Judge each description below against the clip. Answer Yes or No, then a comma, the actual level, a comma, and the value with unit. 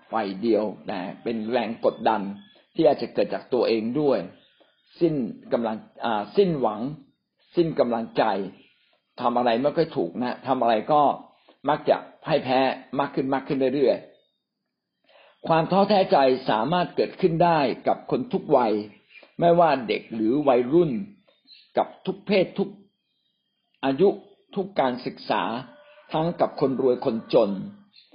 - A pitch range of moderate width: No, wide, 7.8 semitones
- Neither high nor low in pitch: Yes, medium, 145 Hz